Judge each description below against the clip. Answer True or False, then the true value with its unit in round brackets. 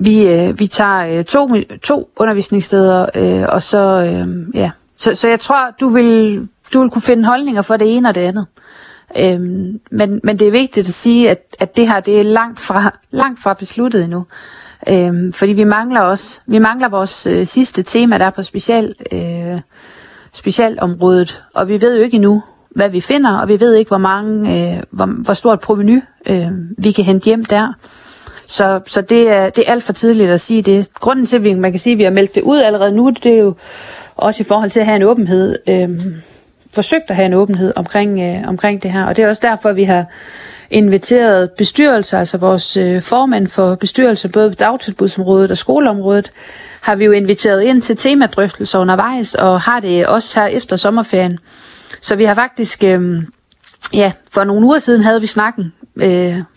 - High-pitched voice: True (205 Hz)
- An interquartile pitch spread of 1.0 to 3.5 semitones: True (3.2 semitones)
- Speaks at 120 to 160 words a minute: False (205 wpm)